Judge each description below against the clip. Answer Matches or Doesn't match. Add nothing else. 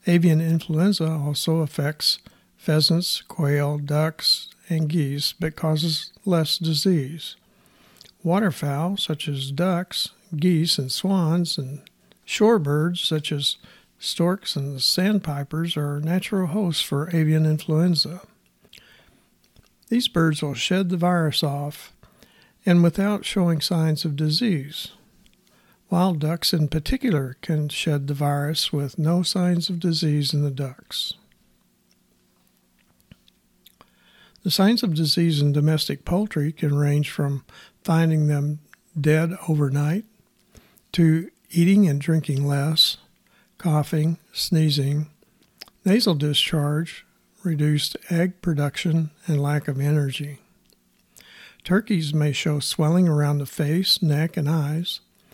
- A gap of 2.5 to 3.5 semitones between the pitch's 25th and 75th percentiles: Matches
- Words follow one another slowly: Matches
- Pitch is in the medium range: Matches